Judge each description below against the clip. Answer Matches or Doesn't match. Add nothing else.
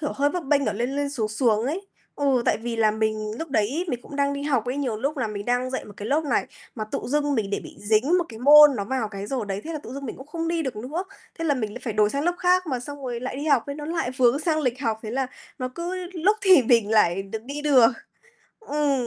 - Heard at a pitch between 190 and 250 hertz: Doesn't match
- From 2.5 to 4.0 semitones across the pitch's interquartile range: Doesn't match